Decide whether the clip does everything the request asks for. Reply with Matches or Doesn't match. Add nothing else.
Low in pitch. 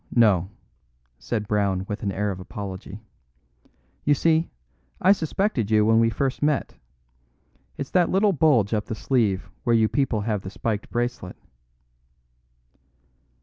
Matches